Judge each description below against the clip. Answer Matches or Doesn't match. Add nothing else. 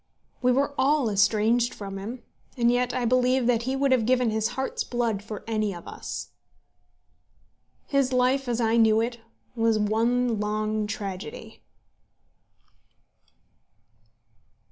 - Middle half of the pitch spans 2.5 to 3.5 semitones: Matches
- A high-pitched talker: Matches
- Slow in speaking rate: Matches